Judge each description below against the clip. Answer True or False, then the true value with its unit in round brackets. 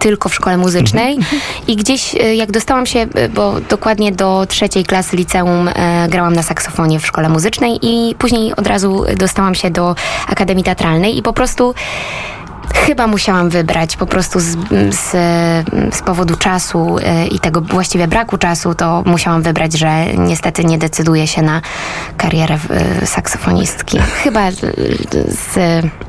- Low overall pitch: False (180 Hz)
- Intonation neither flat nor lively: True (3.8 semitones)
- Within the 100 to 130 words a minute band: False (150 wpm)